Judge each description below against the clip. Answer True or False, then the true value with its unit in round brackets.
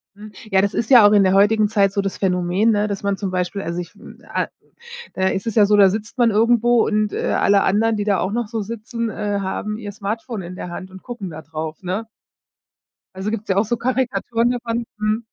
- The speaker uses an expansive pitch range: False (2.9 semitones)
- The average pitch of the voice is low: False (210 Hz)